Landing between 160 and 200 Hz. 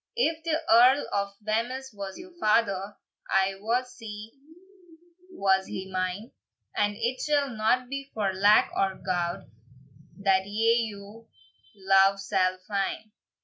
No: high, 210 Hz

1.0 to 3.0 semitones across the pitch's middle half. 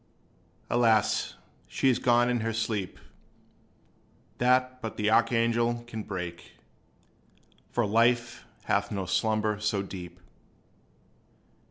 Yes: narrow, 2.5 semitones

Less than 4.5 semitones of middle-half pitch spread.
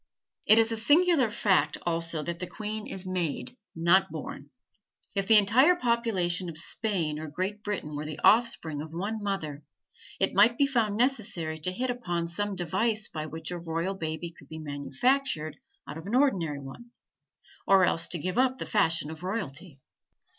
No: wide, 5.5 semitones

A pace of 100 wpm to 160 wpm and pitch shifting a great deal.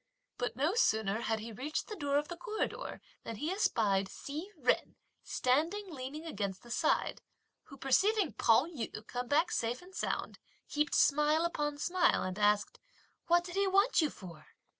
No: average, 170 wpm; wide, 7.3 semitones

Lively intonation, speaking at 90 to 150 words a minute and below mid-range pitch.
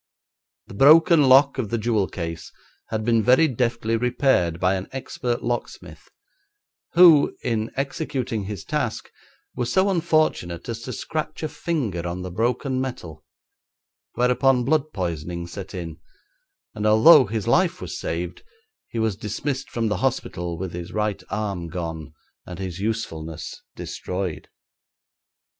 Yes: wide, 6.5 semitones; average, 140 wpm; low, 110 Hz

